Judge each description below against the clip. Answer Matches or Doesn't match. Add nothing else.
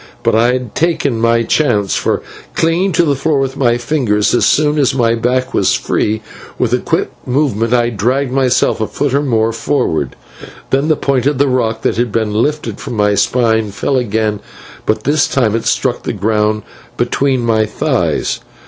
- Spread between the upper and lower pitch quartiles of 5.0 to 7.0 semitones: Doesn't match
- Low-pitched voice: Matches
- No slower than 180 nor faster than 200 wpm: Matches